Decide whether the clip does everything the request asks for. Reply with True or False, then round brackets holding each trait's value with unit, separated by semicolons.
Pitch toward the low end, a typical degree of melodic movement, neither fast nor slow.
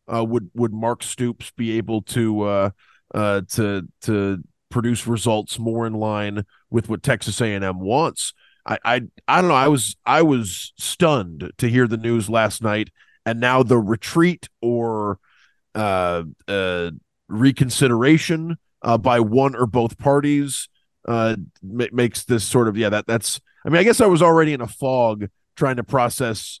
True (115 Hz; 3.5 semitones; 170 wpm)